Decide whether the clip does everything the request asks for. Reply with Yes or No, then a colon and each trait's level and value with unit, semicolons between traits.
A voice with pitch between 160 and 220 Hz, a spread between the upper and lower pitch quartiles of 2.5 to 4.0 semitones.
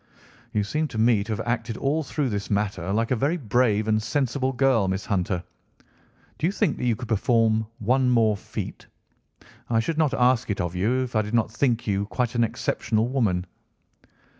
No: low, 115 Hz; average, 3.4 semitones